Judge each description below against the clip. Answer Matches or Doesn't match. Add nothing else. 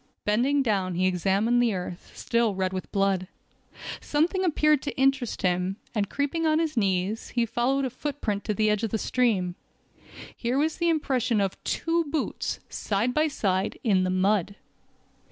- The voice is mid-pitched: Doesn't match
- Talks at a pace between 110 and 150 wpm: Doesn't match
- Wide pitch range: Matches